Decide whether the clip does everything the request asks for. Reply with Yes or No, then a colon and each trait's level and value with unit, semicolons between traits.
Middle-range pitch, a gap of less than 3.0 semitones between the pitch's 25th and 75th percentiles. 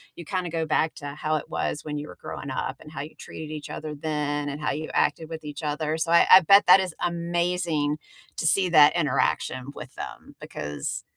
Yes: medium, 155 Hz; narrow, 2.4 semitones